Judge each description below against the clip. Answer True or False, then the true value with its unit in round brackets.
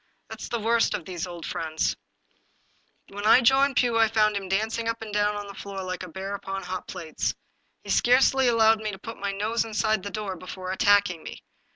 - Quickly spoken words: True (210 wpm)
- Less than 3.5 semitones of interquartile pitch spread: True (3.0 semitones)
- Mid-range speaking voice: False (205 Hz)